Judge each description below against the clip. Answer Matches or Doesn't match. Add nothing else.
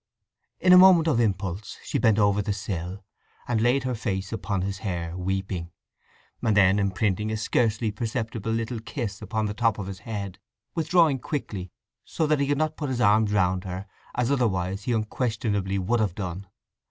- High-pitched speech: Doesn't match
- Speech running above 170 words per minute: Matches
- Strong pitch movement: Doesn't match